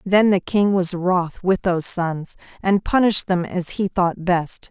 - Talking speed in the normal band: Yes, average, 190 wpm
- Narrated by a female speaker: Yes, female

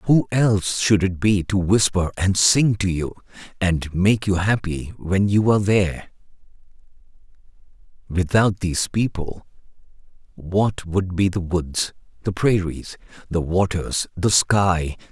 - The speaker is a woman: No, male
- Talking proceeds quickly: No, average, 140 wpm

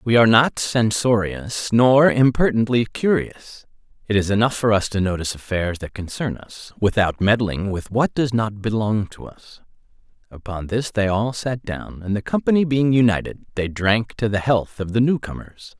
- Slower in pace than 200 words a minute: Yes, average, 180 wpm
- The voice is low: Yes, low, 110 Hz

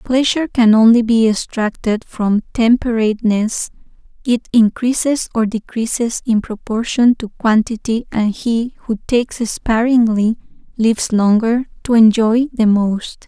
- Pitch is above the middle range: Yes, high, 230 Hz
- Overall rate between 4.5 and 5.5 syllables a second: No, 4.1 syllables/s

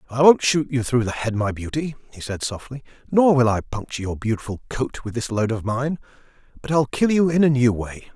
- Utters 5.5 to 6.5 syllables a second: Yes, 5.6 syllables/s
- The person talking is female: No, male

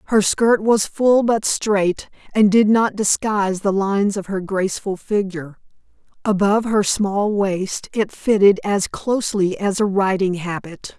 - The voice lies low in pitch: No, high, 200 Hz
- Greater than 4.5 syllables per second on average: No, 4.3 syllables/s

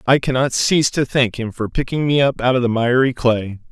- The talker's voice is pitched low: Yes, low, 125 Hz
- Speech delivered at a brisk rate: Yes, fast, 240 wpm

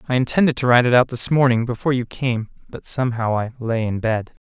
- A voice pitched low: Yes, low, 120 Hz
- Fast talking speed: Yes, fast, 230 wpm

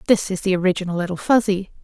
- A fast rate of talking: No, average, 195 wpm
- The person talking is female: Yes, female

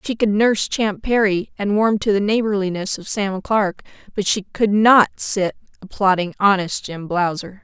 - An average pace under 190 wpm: Yes, average, 175 wpm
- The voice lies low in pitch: No, high, 200 Hz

